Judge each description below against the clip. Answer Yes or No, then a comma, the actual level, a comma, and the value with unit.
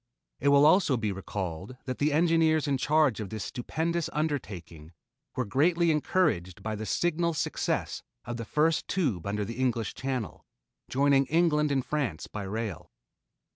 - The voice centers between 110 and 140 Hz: Yes, low, 135 Hz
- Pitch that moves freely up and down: Yes, wide, 6.5 semitones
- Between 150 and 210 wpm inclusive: Yes, average, 155 wpm